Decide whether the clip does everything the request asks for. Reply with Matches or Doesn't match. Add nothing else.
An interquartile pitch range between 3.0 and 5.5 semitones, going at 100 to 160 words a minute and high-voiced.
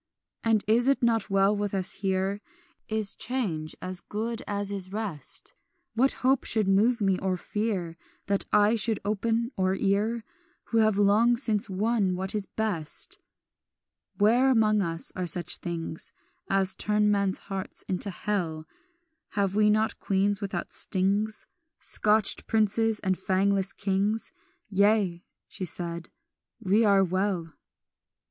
Doesn't match